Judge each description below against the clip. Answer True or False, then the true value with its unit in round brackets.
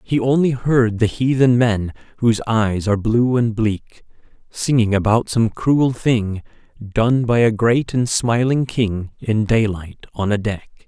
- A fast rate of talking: False (160 wpm)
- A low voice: True (115 Hz)